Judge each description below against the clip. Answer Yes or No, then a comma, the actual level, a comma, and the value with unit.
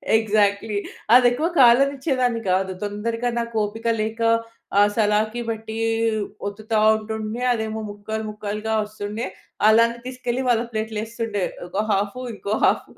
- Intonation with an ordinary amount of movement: No, narrow, 1.9 semitones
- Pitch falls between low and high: No, high, 220 Hz